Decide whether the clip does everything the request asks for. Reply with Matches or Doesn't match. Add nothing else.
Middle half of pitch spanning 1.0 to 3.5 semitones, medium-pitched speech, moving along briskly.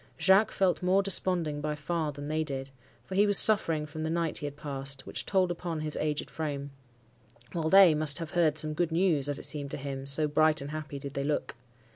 Matches